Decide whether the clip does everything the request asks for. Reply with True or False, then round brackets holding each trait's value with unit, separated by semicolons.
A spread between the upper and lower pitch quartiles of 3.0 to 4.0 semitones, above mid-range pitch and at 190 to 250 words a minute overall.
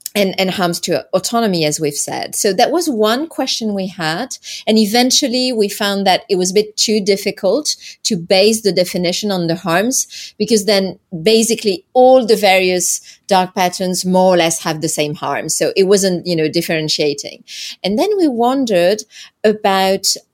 False (3.7 semitones; 195 Hz; 175 wpm)